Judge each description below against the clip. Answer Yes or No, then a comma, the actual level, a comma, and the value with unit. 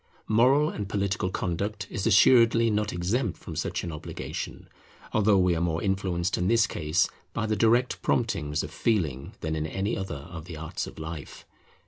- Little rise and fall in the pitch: No, average, 4.8 semitones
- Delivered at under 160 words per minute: No, average, 175 wpm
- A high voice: No, very low, 95 Hz